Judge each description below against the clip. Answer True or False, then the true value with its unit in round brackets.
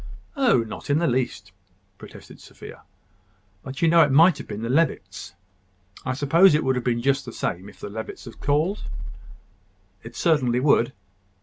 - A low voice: True (130 Hz)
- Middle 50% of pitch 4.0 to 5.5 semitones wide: True (5.2 semitones)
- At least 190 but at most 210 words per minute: False (175 wpm)